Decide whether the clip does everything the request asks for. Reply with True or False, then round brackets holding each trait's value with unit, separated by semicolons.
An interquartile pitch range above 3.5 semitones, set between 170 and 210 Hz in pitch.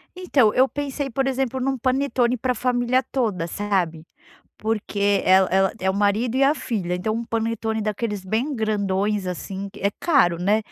False (4.4 semitones; 220 Hz)